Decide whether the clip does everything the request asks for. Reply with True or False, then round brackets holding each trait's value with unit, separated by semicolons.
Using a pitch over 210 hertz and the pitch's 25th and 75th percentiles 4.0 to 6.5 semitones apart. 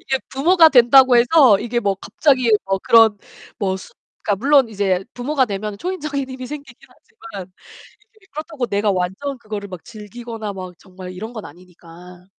True (225 Hz; 5.6 semitones)